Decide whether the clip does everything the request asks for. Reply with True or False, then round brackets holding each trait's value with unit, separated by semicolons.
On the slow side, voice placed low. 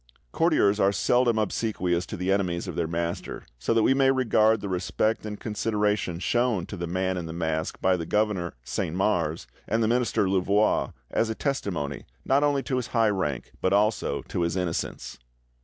False (190 wpm; 100 Hz)